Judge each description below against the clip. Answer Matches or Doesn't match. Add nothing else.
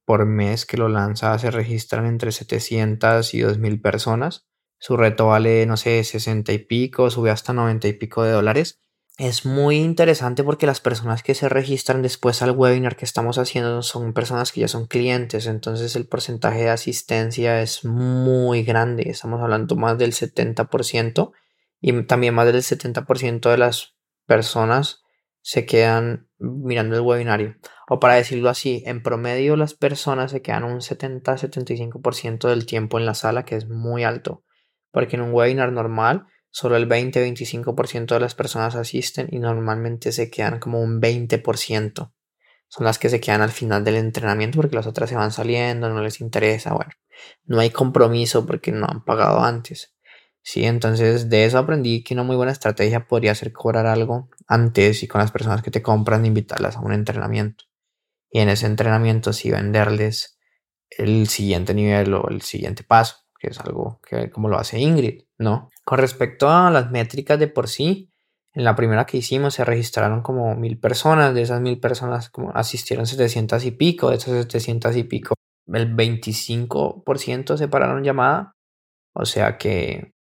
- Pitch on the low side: Matches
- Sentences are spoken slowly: Doesn't match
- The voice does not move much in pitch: Matches